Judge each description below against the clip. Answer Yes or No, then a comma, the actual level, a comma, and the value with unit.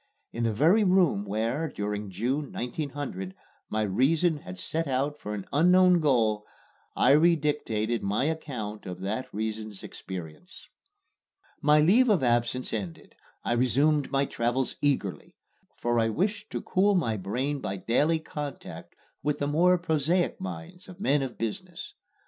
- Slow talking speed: No, average, 145 wpm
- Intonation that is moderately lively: No, wide, 6.6 semitones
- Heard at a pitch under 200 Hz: Yes, low, 135 Hz